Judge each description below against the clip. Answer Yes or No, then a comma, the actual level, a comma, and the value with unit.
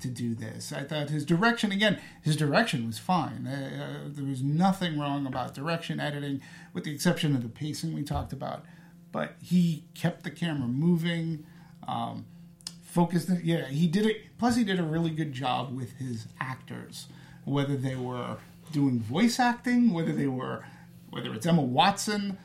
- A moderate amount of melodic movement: Yes, average, 4.0 semitones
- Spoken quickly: No, average, 170 wpm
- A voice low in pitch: No, medium, 160 Hz